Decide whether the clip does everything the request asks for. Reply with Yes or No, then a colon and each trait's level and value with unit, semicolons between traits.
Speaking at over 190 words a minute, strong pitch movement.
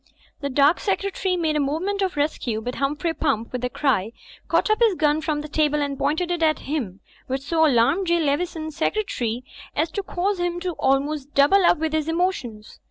No: average, 200 wpm; average, 4.2 semitones